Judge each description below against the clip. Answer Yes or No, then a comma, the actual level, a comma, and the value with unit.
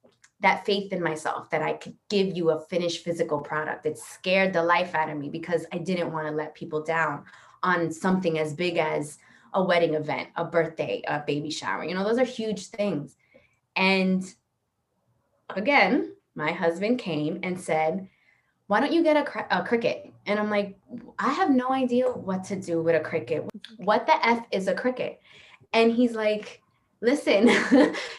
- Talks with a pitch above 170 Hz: Yes, medium, 185 Hz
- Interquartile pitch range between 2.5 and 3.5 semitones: No, average, 5.1 semitones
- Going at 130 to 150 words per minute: No, average, 180 wpm